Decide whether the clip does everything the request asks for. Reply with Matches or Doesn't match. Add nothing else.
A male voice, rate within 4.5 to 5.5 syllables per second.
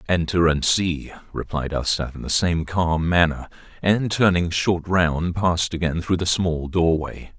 Doesn't match